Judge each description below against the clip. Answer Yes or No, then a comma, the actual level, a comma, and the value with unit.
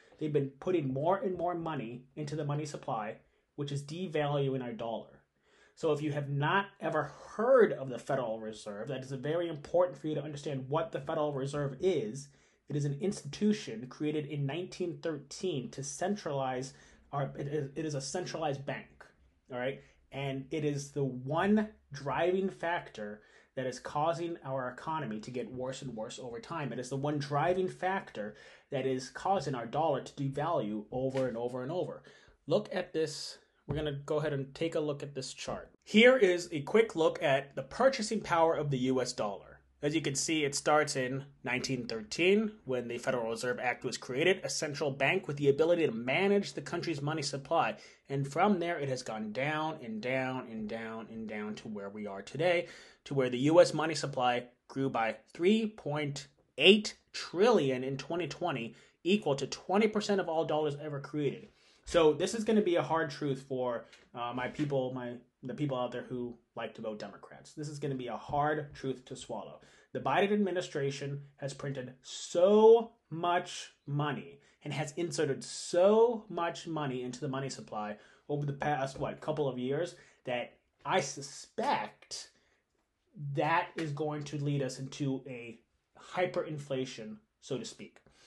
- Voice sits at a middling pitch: Yes, medium, 145 Hz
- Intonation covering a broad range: No, average, 4.2 semitones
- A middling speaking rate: Yes, average, 175 wpm